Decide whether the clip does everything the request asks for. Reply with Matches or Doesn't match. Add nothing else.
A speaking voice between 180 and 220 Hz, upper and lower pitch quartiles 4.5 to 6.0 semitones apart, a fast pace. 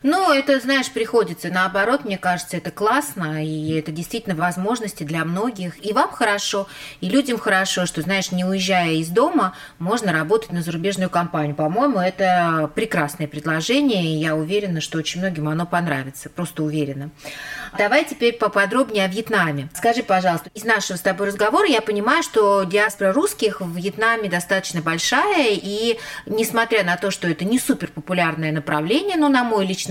Matches